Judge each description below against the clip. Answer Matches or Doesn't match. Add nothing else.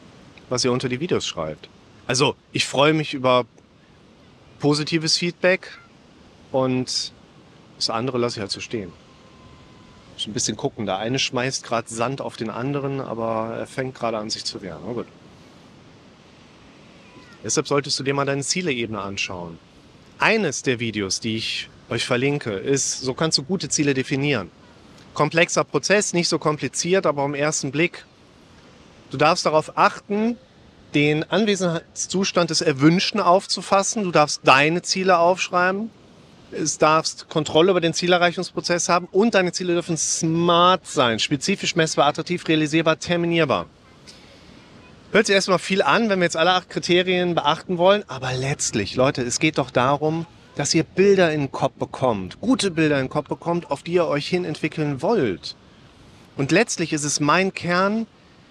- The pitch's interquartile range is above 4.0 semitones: Matches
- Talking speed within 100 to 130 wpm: Doesn't match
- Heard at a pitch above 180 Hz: Doesn't match